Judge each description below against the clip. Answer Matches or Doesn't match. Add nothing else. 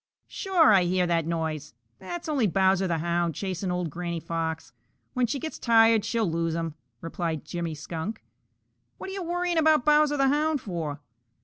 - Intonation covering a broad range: Matches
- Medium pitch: Matches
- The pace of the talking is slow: Doesn't match